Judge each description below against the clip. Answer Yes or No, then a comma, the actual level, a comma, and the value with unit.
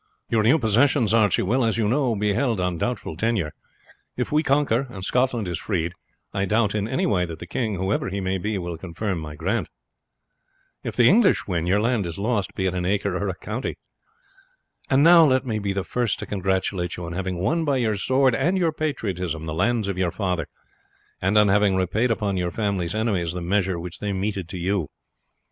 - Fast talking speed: Yes, fast, 210 wpm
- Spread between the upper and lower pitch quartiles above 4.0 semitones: Yes, average, 4.4 semitones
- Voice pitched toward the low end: Yes, low, 100 Hz